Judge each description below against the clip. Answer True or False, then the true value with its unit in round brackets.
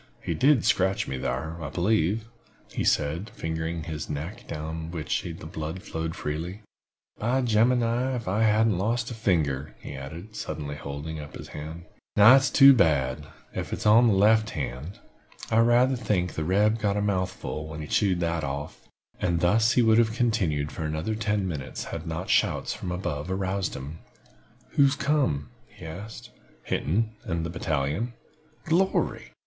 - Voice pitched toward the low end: True (90 Hz)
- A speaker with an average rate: True (170 wpm)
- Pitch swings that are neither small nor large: False (6.1 semitones)